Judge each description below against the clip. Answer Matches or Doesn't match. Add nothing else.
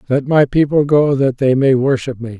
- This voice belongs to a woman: Doesn't match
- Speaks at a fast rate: Matches